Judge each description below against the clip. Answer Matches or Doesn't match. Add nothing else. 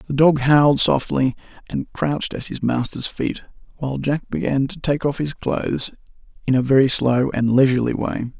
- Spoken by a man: Matches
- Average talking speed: Matches